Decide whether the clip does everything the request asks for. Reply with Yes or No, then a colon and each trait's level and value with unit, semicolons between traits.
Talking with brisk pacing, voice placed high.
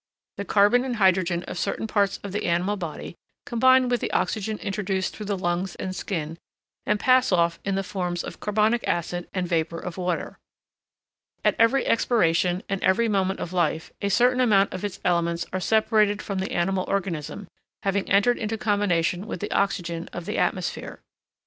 No: average, 180 wpm; high, 195 Hz